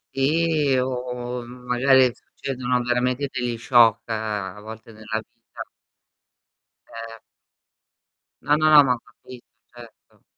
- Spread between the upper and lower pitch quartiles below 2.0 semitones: No, narrow, 2.4 semitones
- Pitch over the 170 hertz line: No, low, 125 Hz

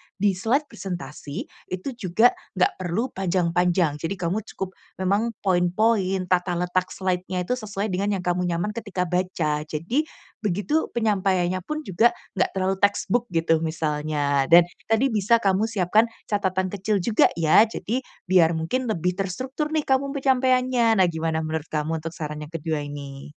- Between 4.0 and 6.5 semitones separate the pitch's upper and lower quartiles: Yes, average, 4.5 semitones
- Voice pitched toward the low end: No, medium, 185 Hz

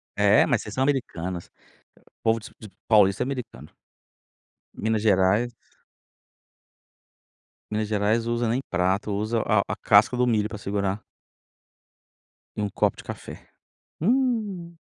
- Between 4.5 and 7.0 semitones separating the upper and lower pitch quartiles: No, average, 3.2 semitones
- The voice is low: Yes, low, 110 Hz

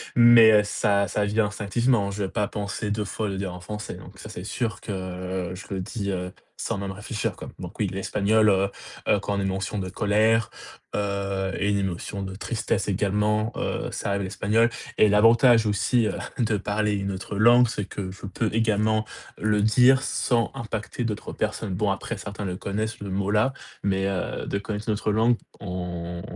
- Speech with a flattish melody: Yes, narrow, 2.0 semitones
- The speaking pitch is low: Yes, low, 105 Hz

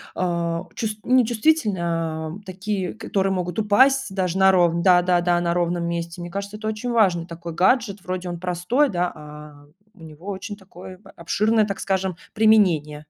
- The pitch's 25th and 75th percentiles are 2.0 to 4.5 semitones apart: Yes, average, 3.4 semitones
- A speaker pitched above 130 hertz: Yes, medium, 185 Hz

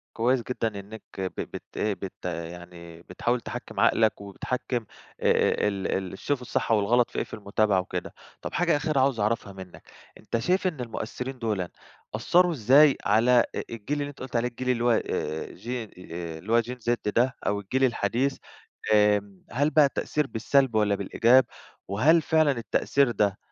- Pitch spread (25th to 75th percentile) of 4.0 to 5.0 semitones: Yes, average, 4.4 semitones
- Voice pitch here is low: Yes, low, 115 Hz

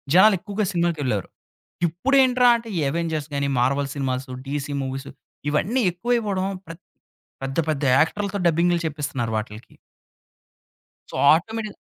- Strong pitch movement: Yes, wide, 6.6 semitones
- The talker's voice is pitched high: No, medium, 165 Hz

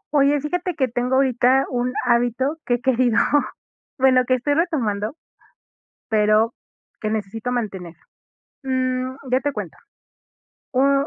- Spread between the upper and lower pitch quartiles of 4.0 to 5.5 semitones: No, average, 2.8 semitones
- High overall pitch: Yes, very high, 255 Hz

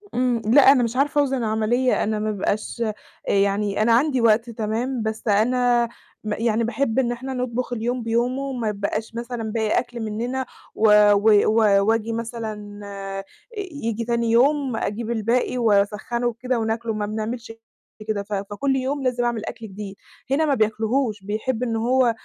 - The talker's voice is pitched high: Yes, high, 230 Hz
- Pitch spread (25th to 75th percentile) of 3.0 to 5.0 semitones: No, narrow, 2.6 semitones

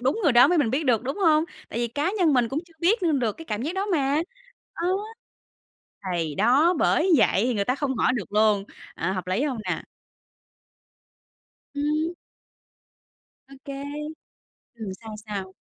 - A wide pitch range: Yes, wide, 6.5 semitones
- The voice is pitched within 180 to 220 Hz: No, very high, 270 Hz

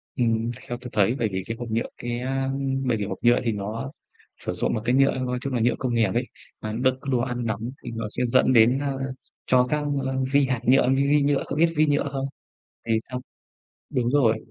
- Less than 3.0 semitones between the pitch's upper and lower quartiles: Yes, narrow, 2.6 semitones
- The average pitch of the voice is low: Yes, low, 125 Hz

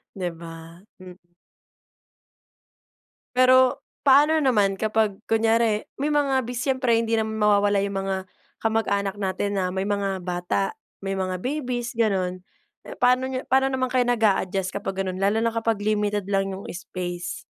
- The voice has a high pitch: Yes, high, 205 Hz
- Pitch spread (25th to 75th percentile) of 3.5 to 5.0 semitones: Yes, average, 4.0 semitones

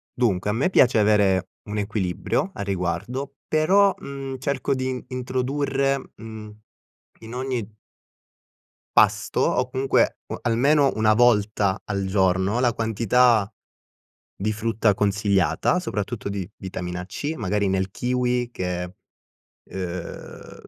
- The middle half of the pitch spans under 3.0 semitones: No, average, 4.6 semitones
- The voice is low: Yes, low, 110 Hz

